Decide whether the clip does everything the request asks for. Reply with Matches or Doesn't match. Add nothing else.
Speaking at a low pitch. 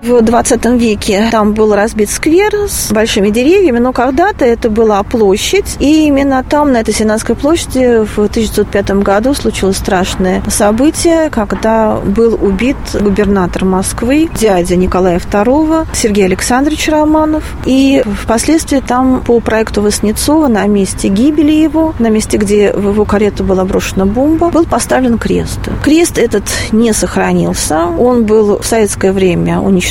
Doesn't match